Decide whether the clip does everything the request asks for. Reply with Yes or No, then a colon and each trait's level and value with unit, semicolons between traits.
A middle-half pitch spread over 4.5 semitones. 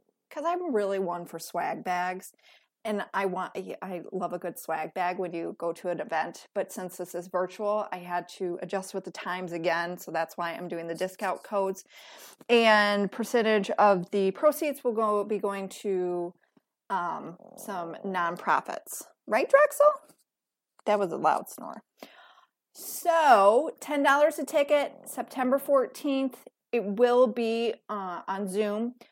Yes: average, 5.1 semitones